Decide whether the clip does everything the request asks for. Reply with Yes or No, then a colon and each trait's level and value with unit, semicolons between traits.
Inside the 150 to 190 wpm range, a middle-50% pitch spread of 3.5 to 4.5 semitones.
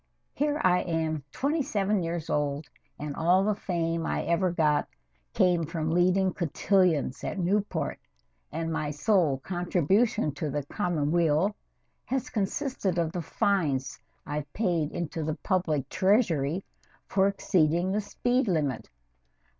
No: slow, 135 wpm; average, 4.1 semitones